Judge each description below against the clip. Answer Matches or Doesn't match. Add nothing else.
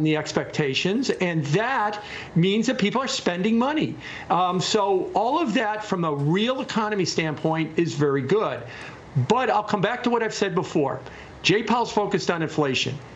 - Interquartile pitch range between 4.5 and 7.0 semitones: Matches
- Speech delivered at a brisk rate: Doesn't match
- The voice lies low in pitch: Doesn't match